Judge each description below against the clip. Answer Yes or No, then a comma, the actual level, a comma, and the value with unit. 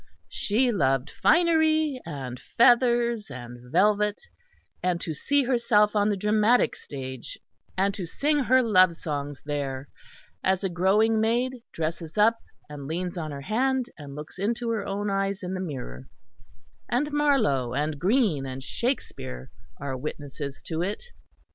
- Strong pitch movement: Yes, wide, 8.4 semitones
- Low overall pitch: No, high, 195 Hz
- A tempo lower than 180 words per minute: Yes, average, 145 wpm